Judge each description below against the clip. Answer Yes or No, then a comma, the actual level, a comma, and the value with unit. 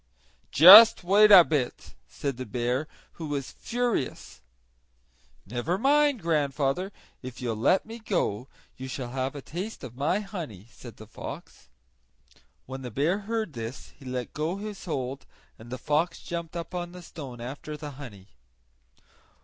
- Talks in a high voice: No, medium, 145 Hz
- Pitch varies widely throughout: Yes, wide, 6.2 semitones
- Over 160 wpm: No, average, 155 wpm